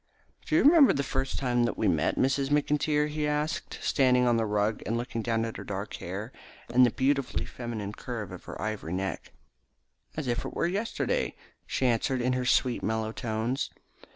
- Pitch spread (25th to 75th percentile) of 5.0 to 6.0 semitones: No, average, 4.0 semitones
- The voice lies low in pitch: Yes, low, 125 Hz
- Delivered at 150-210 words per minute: Yes, average, 190 wpm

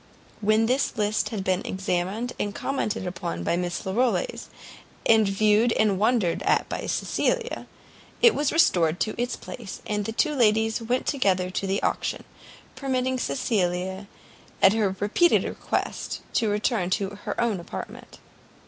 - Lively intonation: No, average, 4.2 semitones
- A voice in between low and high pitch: No, high, 210 Hz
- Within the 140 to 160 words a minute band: Yes, average, 145 wpm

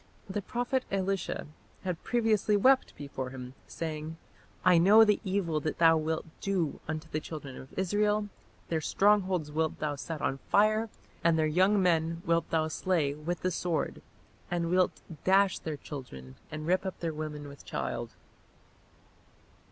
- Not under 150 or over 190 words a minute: Yes, average, 155 wpm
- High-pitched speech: No, medium, 165 Hz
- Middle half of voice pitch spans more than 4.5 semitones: No, average, 4.1 semitones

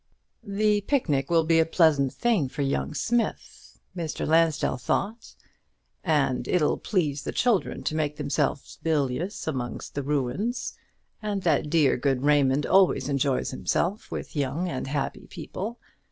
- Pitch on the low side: No, medium, 155 Hz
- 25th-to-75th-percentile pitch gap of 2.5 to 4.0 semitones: No, average, 5.1 semitones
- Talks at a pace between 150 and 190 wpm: No, average, 140 wpm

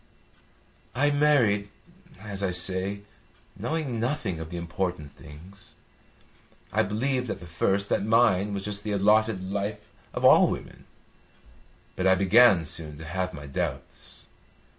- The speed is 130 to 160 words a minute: Yes, average, 140 wpm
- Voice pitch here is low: Yes, low, 100 Hz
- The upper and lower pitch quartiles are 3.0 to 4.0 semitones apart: Yes, average, 3.3 semitones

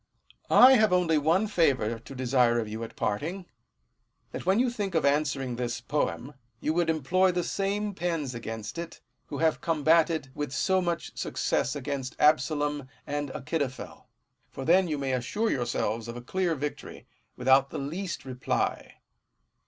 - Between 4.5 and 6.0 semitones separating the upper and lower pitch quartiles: Yes, average, 5.1 semitones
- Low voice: No, medium, 150 Hz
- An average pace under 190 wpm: Yes, average, 160 wpm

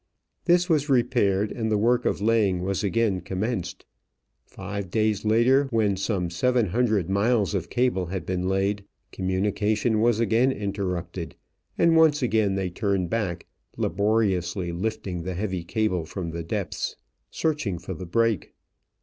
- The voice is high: No, low, 100 Hz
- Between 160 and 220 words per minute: No, average, 145 wpm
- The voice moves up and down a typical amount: Yes, average, 3.8 semitones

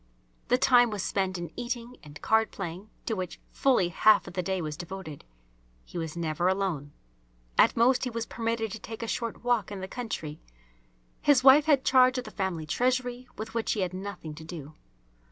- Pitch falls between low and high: No, high, 210 Hz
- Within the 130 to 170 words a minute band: No, average, 195 wpm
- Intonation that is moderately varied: No, wide, 5.7 semitones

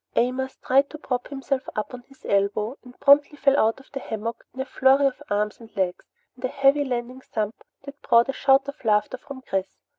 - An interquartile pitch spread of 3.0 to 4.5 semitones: Yes, average, 3.4 semitones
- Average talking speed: No, fast, 215 wpm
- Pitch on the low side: No, very high, 260 Hz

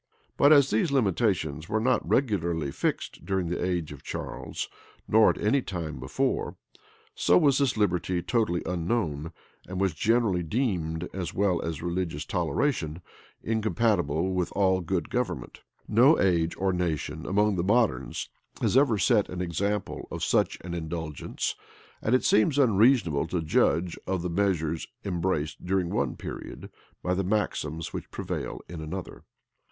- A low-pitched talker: Yes, very low, 90 Hz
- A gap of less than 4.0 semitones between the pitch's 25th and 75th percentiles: No, average, 4.7 semitones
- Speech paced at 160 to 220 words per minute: No, average, 150 wpm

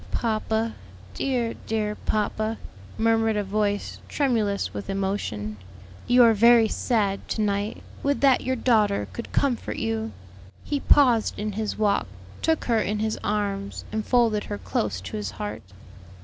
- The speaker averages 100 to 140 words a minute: No, average, 150 wpm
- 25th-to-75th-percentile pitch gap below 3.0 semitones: Yes, narrow, 2.4 semitones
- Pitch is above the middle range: Yes, high, 215 Hz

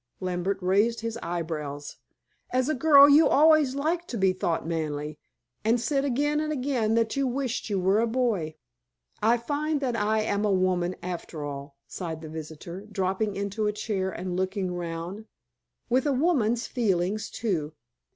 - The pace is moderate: Yes, average, 165 wpm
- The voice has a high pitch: Yes, high, 210 Hz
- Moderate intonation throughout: No, wide, 6.2 semitones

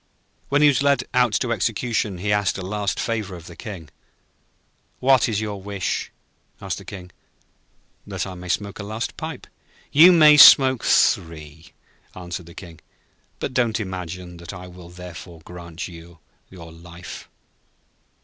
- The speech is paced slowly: No, average, 155 wpm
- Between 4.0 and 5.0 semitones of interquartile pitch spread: Yes, average, 4.5 semitones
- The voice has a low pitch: Yes, very low, 95 Hz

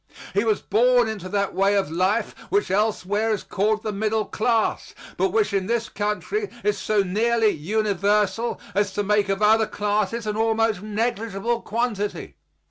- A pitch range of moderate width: No, narrow, 1.9 semitones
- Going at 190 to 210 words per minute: No, average, 160 wpm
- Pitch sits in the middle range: No, high, 215 Hz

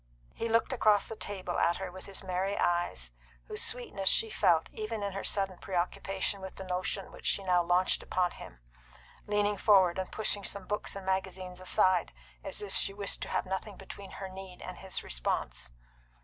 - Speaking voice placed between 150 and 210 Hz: Yes, high, 190 Hz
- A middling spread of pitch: No, narrow, 1.8 semitones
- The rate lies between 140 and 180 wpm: No, average, 190 wpm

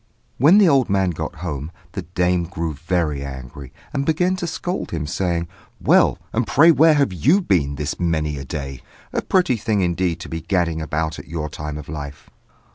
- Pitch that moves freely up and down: Yes, wide, 6.8 semitones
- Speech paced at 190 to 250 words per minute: Yes, average, 195 wpm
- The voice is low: Yes, very low, 85 Hz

